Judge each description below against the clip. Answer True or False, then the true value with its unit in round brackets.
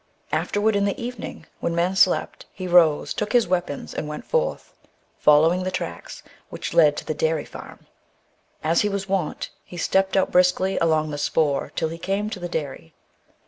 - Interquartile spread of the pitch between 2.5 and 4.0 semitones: True (3.7 semitones)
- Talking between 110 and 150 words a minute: False (185 wpm)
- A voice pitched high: False (175 Hz)